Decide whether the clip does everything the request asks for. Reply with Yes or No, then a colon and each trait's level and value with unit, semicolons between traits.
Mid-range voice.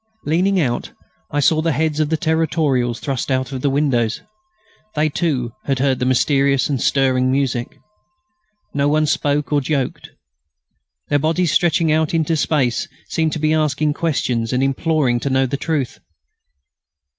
Yes: medium, 145 Hz